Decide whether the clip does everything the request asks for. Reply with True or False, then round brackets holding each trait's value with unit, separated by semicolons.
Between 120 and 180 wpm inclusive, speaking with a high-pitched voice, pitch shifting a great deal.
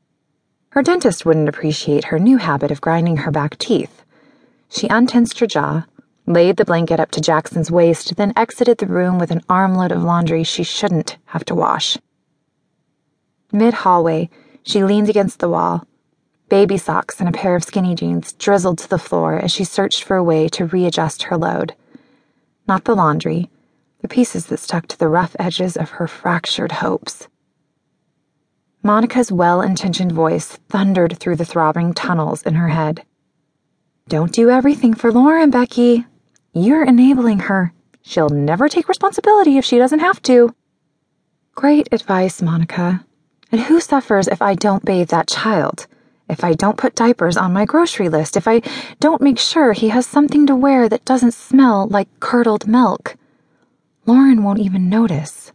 True (165 wpm; 195 Hz; 6.2 semitones)